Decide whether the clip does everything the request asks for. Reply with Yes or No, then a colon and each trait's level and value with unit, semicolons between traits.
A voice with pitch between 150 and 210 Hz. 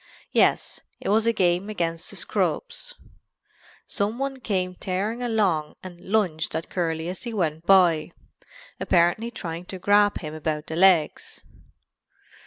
Yes: medium, 185 Hz